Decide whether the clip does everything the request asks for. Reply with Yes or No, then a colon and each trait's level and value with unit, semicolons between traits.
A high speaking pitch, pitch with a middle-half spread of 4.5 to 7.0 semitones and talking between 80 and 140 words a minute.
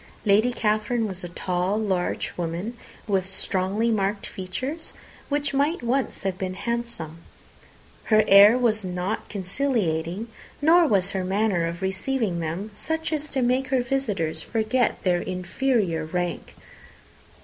Yes: high, 205 Hz; average, 5.0 semitones; slow, 135 wpm